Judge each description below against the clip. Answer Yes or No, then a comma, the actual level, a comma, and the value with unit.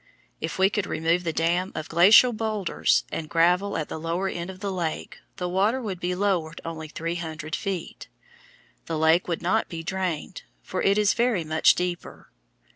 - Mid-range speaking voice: Yes, medium, 175 Hz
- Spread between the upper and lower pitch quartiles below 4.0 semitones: Yes, average, 3.0 semitones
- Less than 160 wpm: No, average, 185 wpm